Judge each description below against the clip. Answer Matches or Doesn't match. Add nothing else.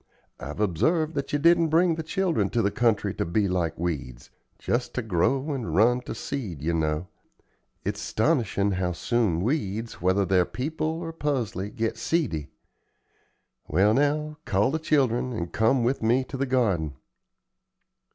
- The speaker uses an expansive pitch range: Matches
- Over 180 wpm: Doesn't match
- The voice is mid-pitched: Doesn't match